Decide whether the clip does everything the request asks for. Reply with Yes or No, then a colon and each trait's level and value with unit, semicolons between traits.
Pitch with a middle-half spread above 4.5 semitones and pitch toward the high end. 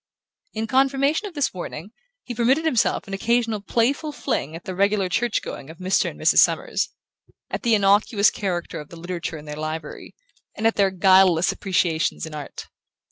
Yes: wide, 5.4 semitones; high, 195 Hz